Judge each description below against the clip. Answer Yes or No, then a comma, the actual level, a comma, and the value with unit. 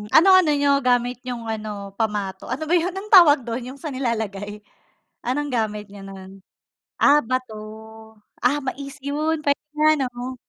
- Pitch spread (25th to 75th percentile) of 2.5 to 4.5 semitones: No, average, 5.2 semitones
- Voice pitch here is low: No, very high, 255 Hz